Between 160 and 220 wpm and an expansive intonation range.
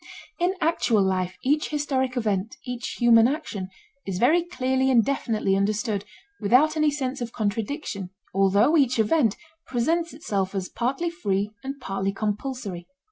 No: average, 140 wpm; wide, 5.7 semitones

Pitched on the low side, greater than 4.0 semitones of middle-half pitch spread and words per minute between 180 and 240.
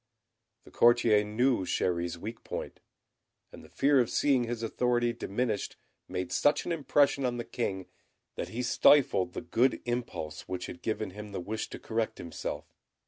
No: low, 115 Hz; average, 4.5 semitones; average, 165 wpm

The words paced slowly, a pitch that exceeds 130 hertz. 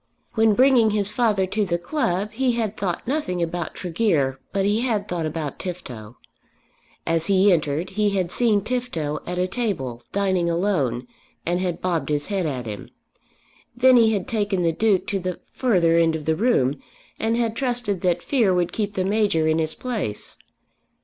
No: average, 180 wpm; high, 190 Hz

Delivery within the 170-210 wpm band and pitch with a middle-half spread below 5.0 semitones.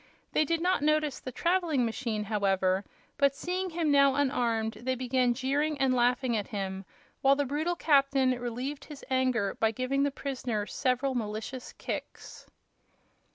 No: average, 155 wpm; average, 3.5 semitones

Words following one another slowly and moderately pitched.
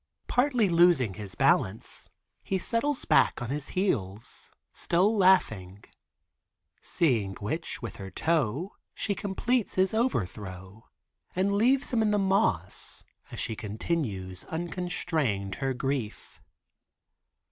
Yes: slow, 115 wpm; medium, 155 Hz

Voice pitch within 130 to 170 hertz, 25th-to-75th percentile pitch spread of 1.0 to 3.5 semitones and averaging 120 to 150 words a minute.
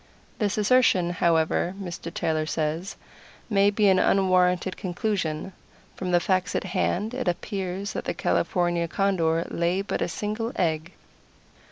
No: medium, 185 Hz; average, 2.7 semitones; average, 140 wpm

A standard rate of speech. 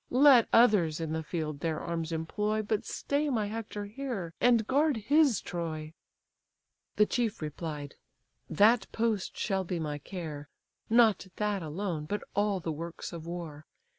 Yes: average, 150 wpm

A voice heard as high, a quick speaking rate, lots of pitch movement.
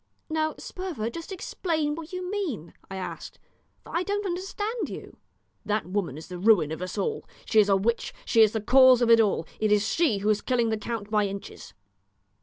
Yes: high, 230 Hz; fast, 210 wpm; wide, 8.5 semitones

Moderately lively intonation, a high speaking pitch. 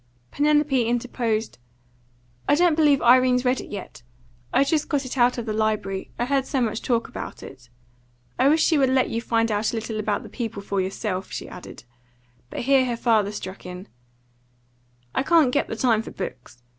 Yes: average, 3.9 semitones; high, 240 Hz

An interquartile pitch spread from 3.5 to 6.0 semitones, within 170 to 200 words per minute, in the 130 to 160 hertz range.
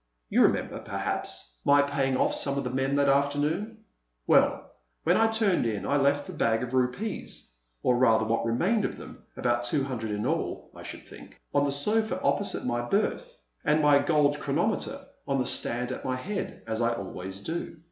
Yes: average, 5.2 semitones; average, 190 wpm; medium, 140 Hz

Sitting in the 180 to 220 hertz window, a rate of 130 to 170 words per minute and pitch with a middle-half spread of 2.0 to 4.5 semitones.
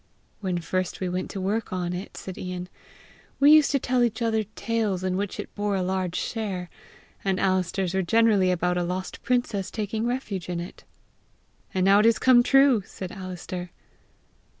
No: high, 190 Hz; average, 180 wpm; average, 3.6 semitones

